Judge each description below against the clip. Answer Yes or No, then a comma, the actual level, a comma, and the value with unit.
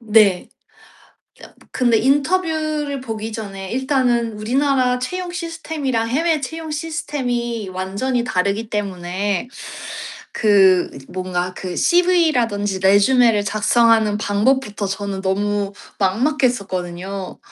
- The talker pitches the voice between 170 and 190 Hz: No, high, 225 Hz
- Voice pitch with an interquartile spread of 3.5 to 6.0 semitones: Yes, average, 5.3 semitones